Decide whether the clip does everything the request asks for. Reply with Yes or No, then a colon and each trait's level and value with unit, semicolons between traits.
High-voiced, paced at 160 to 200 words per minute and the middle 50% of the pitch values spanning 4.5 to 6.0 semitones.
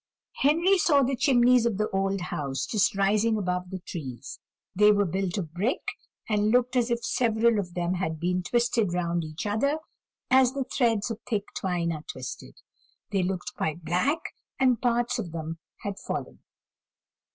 Yes: high, 205 Hz; average, 170 wpm; average, 5.3 semitones